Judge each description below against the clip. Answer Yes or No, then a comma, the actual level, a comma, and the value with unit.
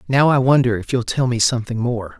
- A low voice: Yes, low, 120 Hz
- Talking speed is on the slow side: No, fast, 245 wpm